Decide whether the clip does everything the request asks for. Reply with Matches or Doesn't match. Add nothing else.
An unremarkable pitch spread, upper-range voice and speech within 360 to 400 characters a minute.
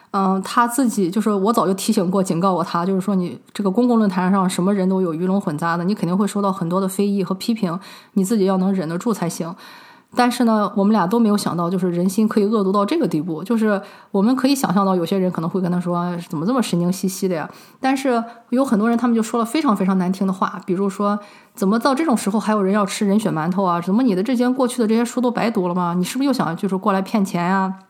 Matches